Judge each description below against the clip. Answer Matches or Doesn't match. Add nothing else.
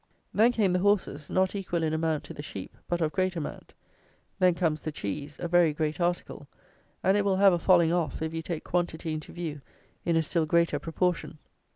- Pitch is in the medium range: Matches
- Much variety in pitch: Doesn't match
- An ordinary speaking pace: Doesn't match